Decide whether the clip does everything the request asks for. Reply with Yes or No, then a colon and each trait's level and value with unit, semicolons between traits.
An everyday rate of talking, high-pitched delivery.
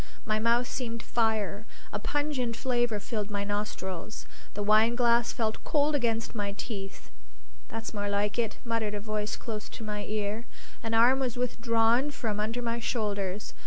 Yes: average, 160 wpm; high, 225 Hz